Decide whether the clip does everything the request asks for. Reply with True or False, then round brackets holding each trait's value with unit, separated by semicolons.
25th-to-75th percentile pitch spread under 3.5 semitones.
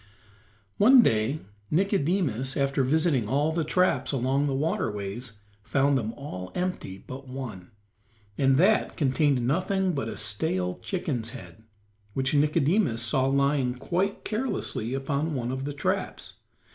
False (4.8 semitones)